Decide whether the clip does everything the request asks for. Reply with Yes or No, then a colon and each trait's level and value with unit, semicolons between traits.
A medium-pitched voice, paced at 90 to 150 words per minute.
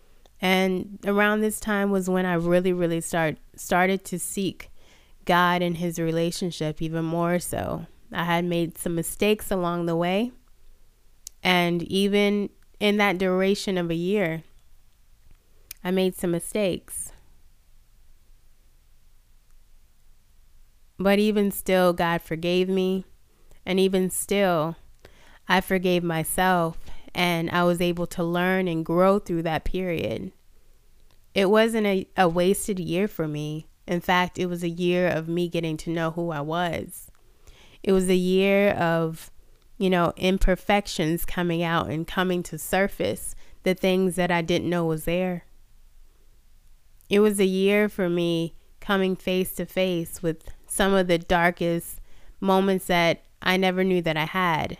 Yes: medium, 180 Hz; average, 140 wpm